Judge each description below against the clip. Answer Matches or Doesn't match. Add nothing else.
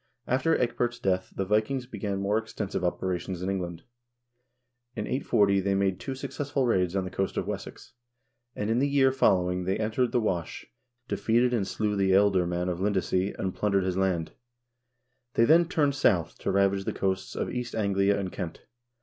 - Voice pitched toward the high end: Doesn't match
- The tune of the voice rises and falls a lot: Doesn't match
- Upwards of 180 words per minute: Doesn't match